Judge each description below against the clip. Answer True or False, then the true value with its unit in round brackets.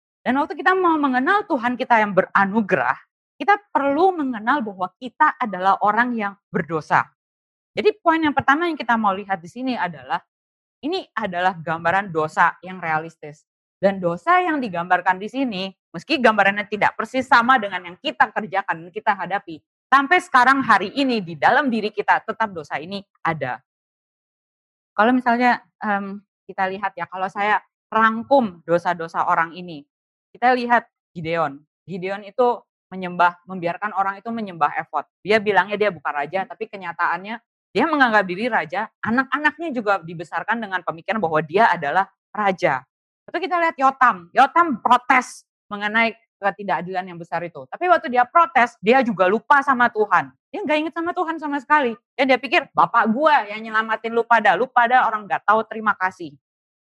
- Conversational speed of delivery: False (160 wpm)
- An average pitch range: False (6.0 semitones)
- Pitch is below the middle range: False (215 Hz)